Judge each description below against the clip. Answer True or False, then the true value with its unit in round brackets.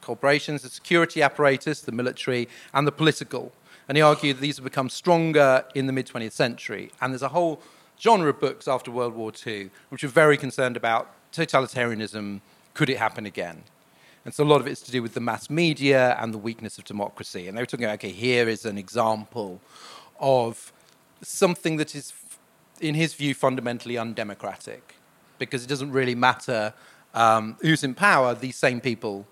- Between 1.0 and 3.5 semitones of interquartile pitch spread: False (3.9 semitones)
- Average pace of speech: True (185 wpm)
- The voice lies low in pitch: True (130 Hz)